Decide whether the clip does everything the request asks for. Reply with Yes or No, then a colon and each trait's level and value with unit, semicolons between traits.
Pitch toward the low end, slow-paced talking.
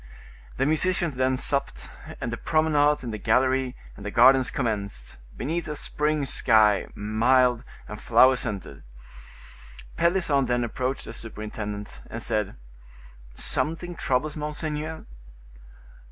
Yes: low, 130 Hz; slow, 120 wpm